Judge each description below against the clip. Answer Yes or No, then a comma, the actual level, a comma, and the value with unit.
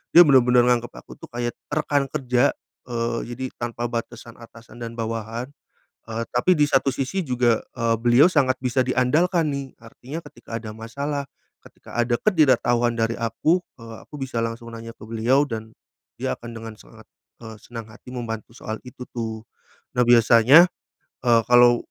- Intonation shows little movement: Yes, narrow, 2.3 semitones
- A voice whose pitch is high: No, low, 120 Hz